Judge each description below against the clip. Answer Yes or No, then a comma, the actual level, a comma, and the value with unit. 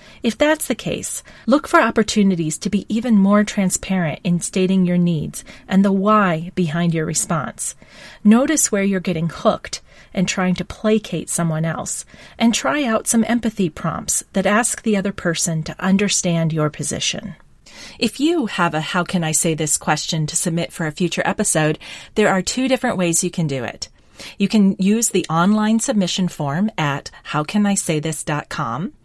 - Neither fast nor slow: Yes, average, 170 wpm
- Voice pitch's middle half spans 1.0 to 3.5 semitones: No, average, 4.4 semitones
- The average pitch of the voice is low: No, high, 190 Hz